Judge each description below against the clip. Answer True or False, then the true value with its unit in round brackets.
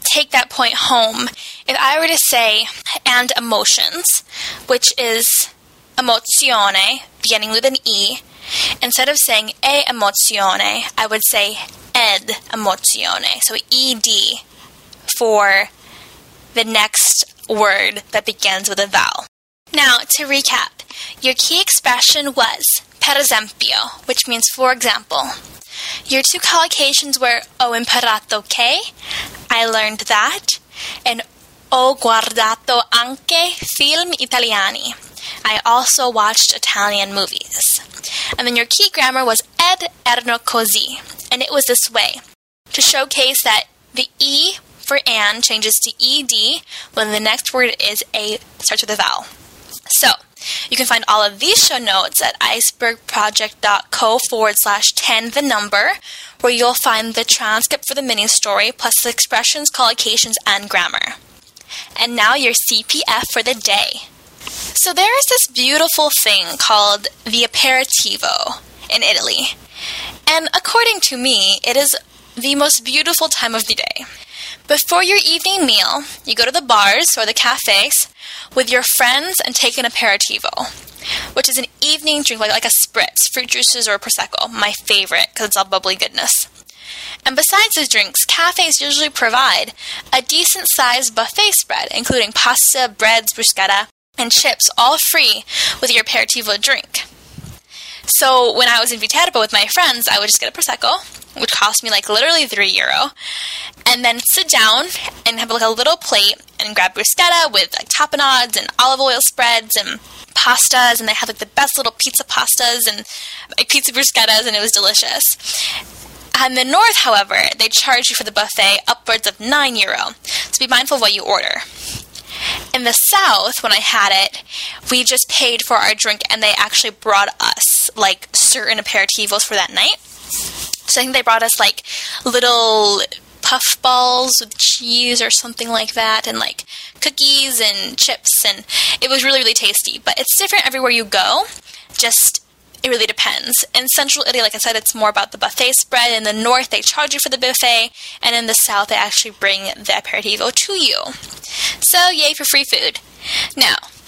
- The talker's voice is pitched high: True (245 Hz)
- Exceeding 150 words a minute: True (160 wpm)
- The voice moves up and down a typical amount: True (4.1 semitones)